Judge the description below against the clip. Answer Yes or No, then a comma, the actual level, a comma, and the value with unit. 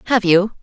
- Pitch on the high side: Yes, high, 200 Hz